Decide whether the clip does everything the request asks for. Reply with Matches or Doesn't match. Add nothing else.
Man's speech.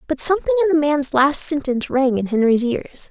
Doesn't match